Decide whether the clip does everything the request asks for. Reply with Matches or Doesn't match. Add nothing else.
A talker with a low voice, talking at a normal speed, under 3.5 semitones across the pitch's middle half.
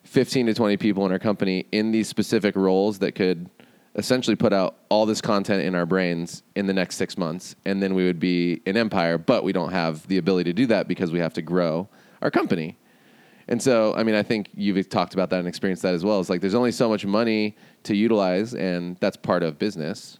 Doesn't match